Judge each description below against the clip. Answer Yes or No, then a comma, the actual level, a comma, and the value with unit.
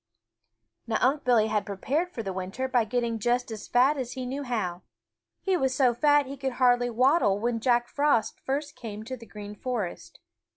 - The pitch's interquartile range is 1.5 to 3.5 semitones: Yes, average, 3.2 semitones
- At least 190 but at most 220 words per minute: Yes, average, 200 wpm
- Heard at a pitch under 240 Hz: No, high, 245 Hz